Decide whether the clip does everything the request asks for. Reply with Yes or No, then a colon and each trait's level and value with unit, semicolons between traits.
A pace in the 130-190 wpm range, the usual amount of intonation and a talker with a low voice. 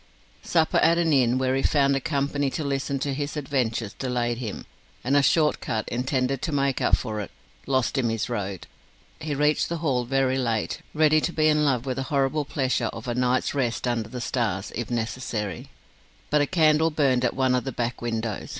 No: fast, 205 wpm; average, 3.3 semitones; low, 130 Hz